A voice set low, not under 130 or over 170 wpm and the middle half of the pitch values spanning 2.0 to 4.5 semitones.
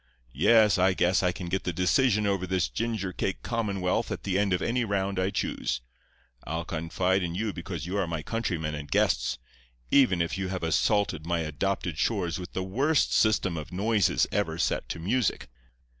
No: very low, 95 Hz; average, 190 wpm; average, 3.3 semitones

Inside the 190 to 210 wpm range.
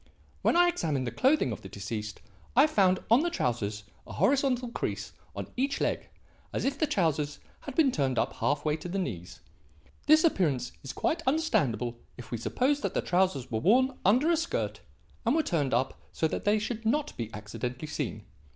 Yes: average, 195 wpm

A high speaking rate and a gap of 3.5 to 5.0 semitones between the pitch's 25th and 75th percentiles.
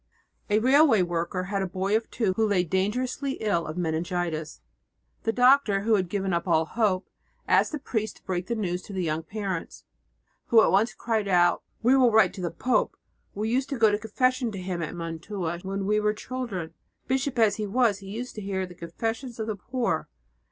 Yes: fast, 210 wpm; average, 4.1 semitones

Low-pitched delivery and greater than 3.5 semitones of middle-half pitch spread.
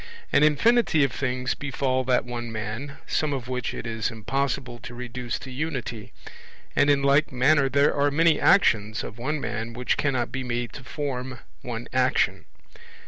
No: low, 130 Hz; average, 2.8 semitones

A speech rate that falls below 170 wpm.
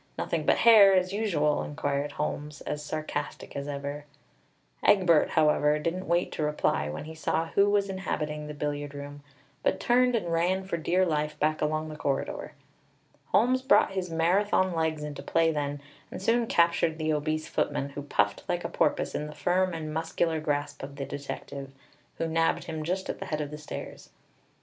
No: average, 185 wpm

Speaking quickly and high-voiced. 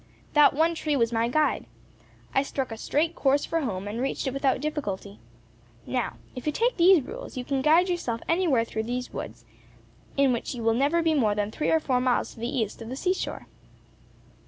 Yes: fast, 210 wpm; very high, 270 Hz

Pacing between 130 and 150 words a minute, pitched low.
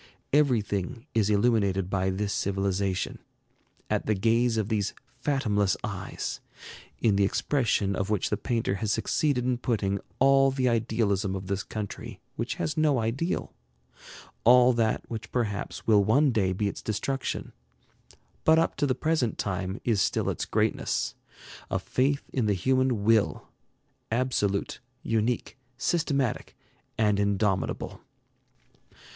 Yes: slow, 135 wpm; low, 110 Hz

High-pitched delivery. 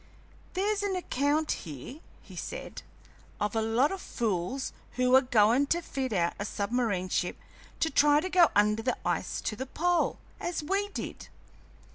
Yes: very high, 260 Hz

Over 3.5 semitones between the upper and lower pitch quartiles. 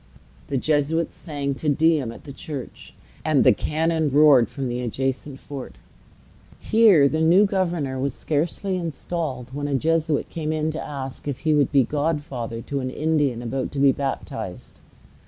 No: average, 3.1 semitones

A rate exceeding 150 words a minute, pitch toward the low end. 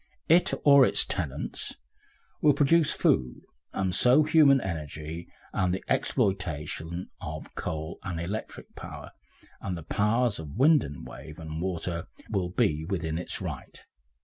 No: average, 140 wpm; very low, 90 Hz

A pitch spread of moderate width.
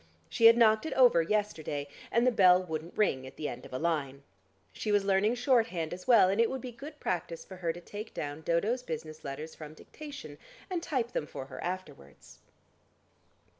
No: wide, 6.7 semitones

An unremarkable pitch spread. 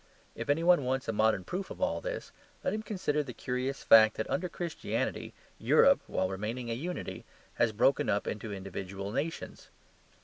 No: wide, 7.4 semitones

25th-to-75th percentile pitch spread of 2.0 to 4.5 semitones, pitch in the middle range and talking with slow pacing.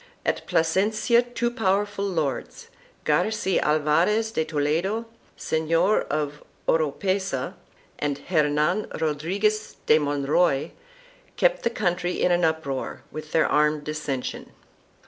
No: average, 5.1 semitones; medium, 165 Hz; slow, 105 wpm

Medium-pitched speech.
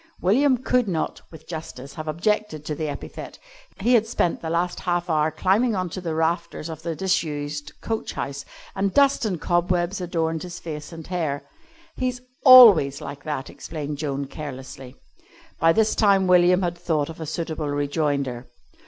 Yes: medium, 165 Hz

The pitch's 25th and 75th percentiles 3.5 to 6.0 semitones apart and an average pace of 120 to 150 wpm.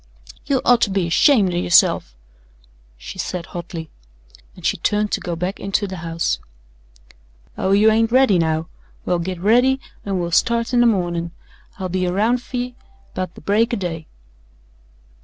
No: average, 4.9 semitones; average, 165 wpm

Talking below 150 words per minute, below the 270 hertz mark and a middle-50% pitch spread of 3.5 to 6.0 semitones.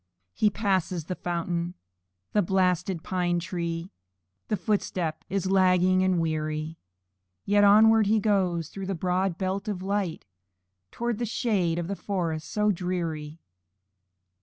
No: slow, 135 wpm; medium, 185 Hz; average, 2.8 semitones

